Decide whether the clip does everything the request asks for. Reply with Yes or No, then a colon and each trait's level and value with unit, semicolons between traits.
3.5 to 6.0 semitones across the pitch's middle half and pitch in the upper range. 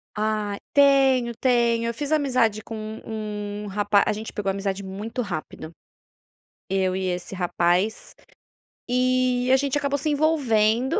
Yes: average, 4.0 semitones; high, 220 Hz